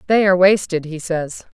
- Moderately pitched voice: Yes, medium, 180 Hz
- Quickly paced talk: No, average, 190 wpm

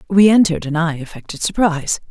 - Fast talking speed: No, average, 170 wpm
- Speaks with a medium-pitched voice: Yes, medium, 170 Hz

